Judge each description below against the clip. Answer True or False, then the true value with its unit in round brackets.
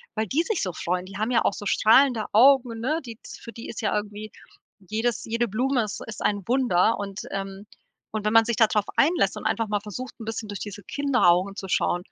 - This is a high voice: True (220 Hz)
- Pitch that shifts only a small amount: False (3.0 semitones)